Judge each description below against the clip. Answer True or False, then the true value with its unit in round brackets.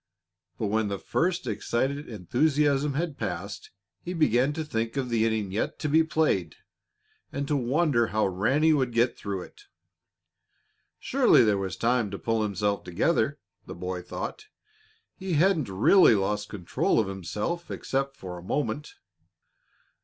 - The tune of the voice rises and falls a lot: True (6.7 semitones)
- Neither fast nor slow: True (150 wpm)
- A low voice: True (120 Hz)